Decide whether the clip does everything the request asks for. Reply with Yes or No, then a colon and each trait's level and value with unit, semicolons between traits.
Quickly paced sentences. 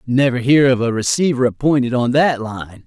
No: average, 190 wpm